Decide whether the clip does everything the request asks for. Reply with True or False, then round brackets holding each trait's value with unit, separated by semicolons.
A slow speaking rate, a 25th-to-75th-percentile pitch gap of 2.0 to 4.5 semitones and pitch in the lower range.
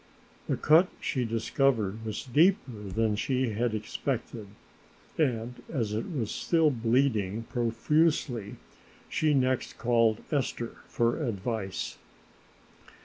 True (105 wpm; 3.7 semitones; 120 Hz)